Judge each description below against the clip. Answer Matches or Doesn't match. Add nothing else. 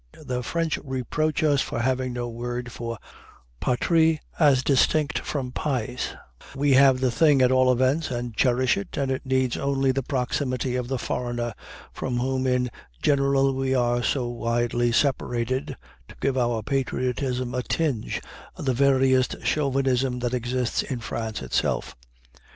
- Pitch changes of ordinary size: Doesn't match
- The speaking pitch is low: Matches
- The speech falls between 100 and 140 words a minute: Doesn't match